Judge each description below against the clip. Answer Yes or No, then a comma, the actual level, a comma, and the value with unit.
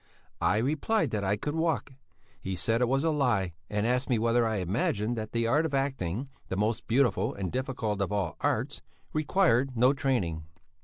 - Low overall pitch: Yes, low, 115 Hz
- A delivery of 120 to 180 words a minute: No, average, 190 wpm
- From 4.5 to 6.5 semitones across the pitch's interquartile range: Yes, average, 4.8 semitones